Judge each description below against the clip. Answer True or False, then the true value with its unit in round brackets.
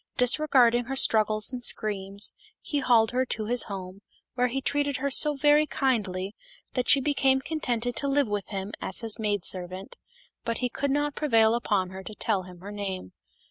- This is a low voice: False (230 Hz)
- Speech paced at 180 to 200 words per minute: True (185 wpm)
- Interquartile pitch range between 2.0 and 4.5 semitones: False (5.0 semitones)